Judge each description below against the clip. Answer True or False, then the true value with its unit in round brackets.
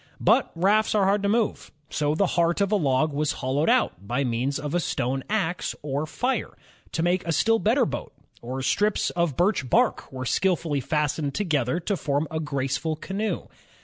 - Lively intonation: True (6.0 semitones)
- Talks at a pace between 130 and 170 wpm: False (190 wpm)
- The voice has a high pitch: False (160 Hz)